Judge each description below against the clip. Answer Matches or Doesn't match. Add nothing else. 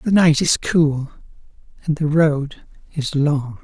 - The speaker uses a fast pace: Doesn't match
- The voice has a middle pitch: Matches